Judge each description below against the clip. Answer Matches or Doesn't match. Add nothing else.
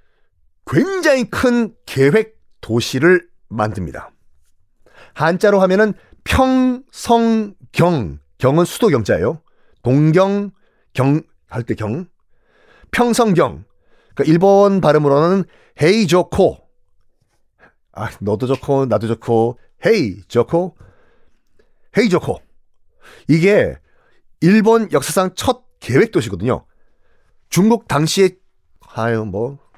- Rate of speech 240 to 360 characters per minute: Doesn't match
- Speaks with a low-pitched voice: Doesn't match